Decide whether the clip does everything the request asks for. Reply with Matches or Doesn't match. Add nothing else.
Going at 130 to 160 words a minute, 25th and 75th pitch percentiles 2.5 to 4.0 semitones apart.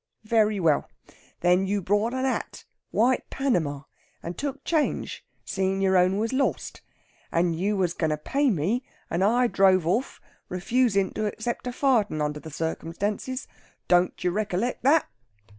Doesn't match